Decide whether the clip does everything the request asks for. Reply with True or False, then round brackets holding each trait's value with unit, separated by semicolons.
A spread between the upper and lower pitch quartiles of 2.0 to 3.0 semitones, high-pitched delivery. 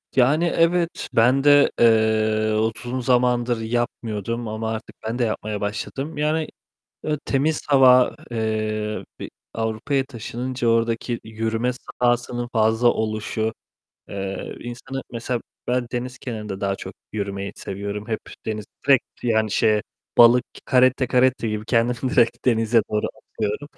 False (2.6 semitones; 115 Hz)